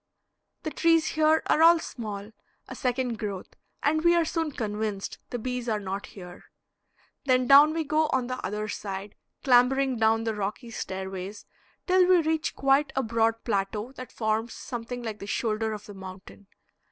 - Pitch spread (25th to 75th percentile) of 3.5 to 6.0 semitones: Yes, average, 5.0 semitones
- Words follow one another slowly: No, average, 170 wpm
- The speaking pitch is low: No, high, 235 Hz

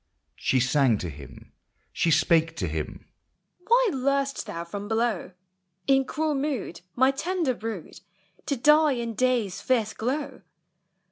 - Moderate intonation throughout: No, wide, 8.6 semitones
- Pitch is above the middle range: Yes, high, 235 Hz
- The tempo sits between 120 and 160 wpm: Yes, average, 140 wpm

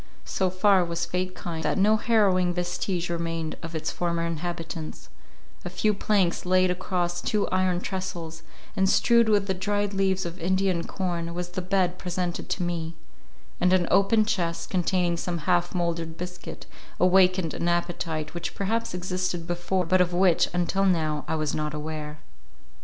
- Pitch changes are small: Yes, narrow, 1.9 semitones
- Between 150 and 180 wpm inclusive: Yes, average, 165 wpm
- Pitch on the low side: No, medium, 180 Hz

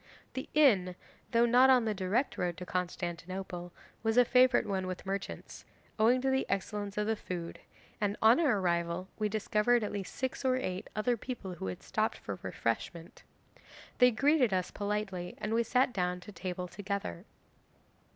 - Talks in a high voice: Yes, high, 205 Hz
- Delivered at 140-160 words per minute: No, average, 170 wpm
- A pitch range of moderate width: Yes, average, 4.9 semitones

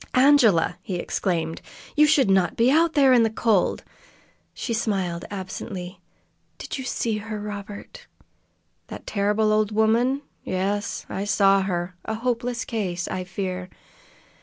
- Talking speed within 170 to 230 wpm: No, slow, 135 wpm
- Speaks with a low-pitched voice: No, high, 210 Hz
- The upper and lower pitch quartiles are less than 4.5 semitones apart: Yes, average, 3.9 semitones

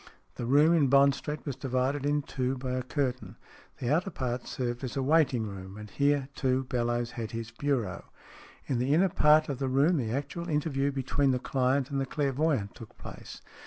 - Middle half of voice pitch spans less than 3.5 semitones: Yes, average, 2.8 semitones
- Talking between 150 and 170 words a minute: No, average, 200 wpm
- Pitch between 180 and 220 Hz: No, low, 135 Hz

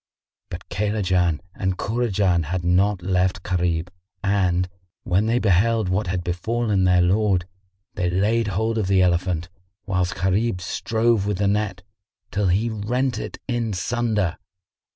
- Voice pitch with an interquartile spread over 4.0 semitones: No, average, 3.1 semitones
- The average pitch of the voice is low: Yes, very low, 95 Hz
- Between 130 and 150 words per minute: Yes, average, 140 wpm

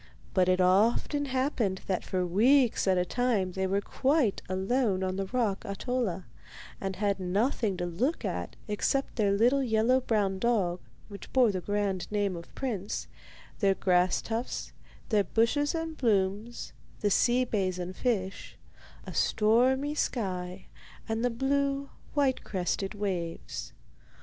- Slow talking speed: No, average, 145 wpm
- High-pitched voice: Yes, high, 205 Hz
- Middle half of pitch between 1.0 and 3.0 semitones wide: No, average, 4.8 semitones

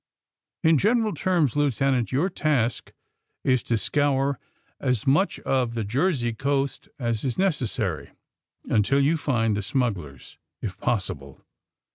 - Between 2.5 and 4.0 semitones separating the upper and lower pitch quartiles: No, average, 4.4 semitones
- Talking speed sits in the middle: No, slow, 125 wpm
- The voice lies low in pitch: Yes, low, 130 Hz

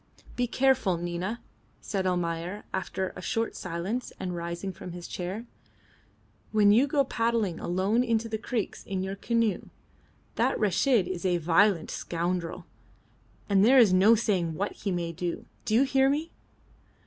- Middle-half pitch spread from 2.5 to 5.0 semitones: Yes, average, 4.5 semitones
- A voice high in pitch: Yes, high, 195 Hz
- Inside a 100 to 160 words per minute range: Yes, average, 155 wpm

